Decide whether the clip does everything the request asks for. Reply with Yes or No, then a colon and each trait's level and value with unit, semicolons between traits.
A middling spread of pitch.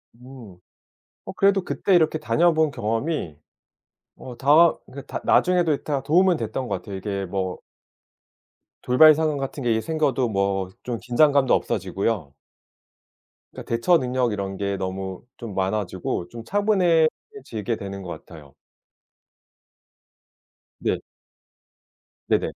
No: wide, 8.1 semitones